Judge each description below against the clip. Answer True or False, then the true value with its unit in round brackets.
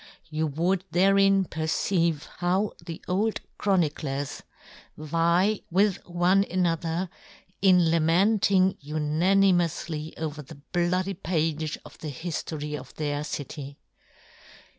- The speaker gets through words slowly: True (110 wpm)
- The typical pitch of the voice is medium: True (170 Hz)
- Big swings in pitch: False (3.3 semitones)